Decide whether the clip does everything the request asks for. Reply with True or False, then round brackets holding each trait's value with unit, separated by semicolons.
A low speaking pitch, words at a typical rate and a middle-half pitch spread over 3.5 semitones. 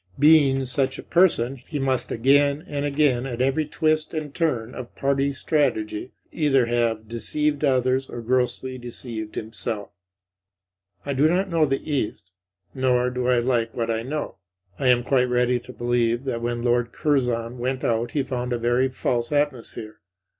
False (125 Hz; 165 wpm; 2.9 semitones)